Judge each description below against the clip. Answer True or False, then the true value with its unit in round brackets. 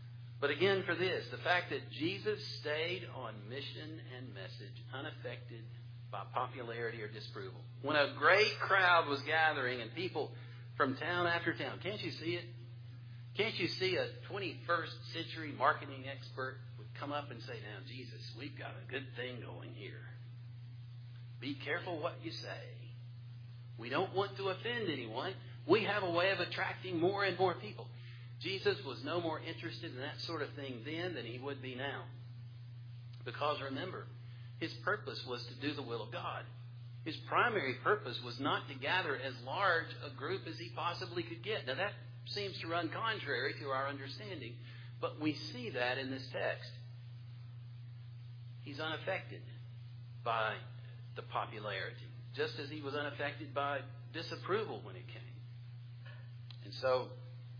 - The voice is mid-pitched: False (120 Hz)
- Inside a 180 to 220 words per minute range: False (160 wpm)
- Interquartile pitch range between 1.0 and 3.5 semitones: True (2.5 semitones)